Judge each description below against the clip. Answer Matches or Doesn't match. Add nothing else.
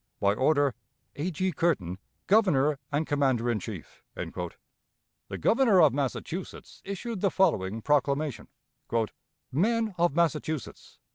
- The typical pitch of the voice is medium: Matches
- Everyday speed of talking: Doesn't match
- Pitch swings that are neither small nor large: Doesn't match